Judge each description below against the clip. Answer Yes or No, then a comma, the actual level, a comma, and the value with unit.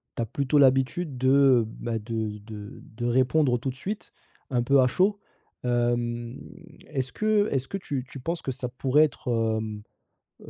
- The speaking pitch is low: Yes, low, 130 Hz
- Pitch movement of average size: Yes, average, 3.0 semitones